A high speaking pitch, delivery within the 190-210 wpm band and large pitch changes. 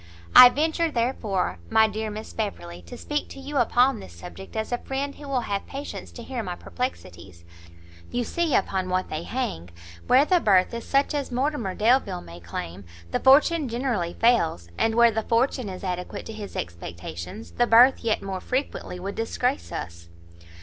No: high, 225 Hz; average, 180 wpm; wide, 6.7 semitones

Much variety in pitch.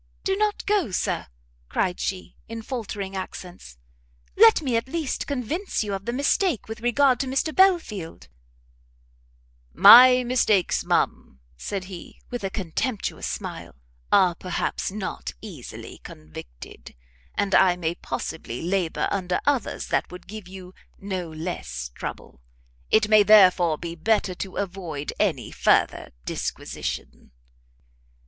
Yes: wide, 5.8 semitones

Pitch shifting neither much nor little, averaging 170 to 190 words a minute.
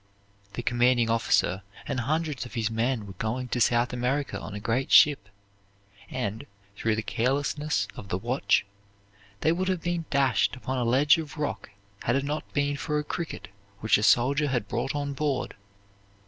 Yes: average, 4.0 semitones; average, 175 wpm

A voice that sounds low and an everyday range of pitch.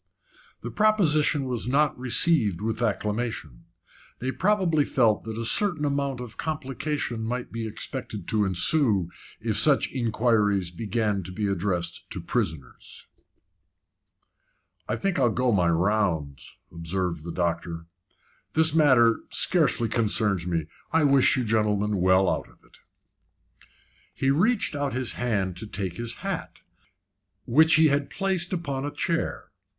No: low, 115 Hz; wide, 6.5 semitones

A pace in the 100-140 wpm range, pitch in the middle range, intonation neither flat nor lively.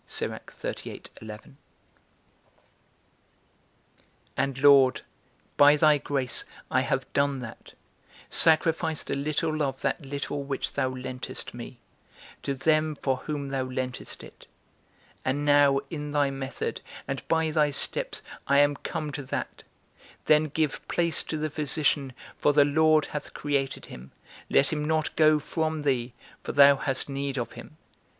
No: slow, 135 wpm; medium, 145 Hz; narrow, 2.1 semitones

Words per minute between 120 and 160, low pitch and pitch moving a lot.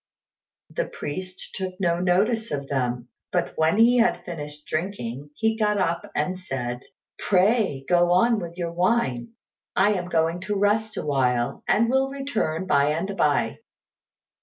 No: average, 150 wpm; medium, 180 Hz; wide, 6.0 semitones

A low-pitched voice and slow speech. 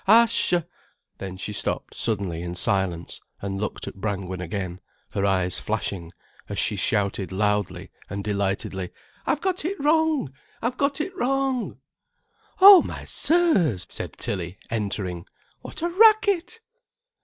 Yes: low, 105 Hz; slow, 130 wpm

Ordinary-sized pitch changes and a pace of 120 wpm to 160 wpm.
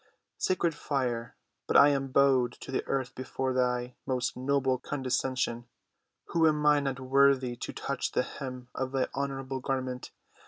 No: narrow, 1.6 semitones; average, 150 wpm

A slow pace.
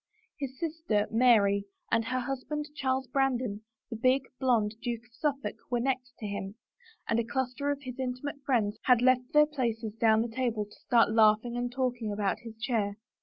No: average, 185 wpm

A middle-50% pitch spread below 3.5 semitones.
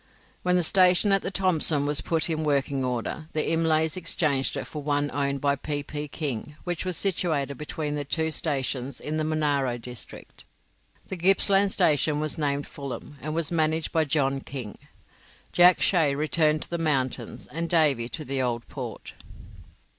Yes: average, 2.8 semitones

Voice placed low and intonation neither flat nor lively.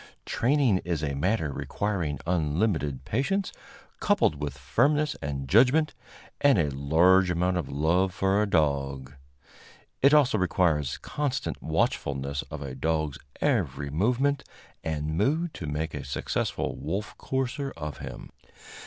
No: very low, 85 Hz; wide, 8.6 semitones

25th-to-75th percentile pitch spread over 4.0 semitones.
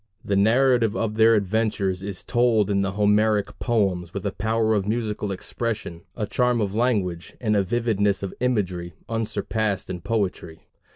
No: narrow, 2.6 semitones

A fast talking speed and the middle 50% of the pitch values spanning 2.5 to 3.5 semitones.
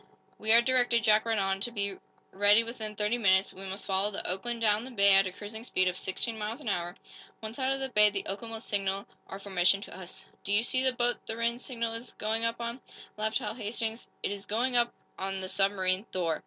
Yes: fast, 235 wpm; average, 3.1 semitones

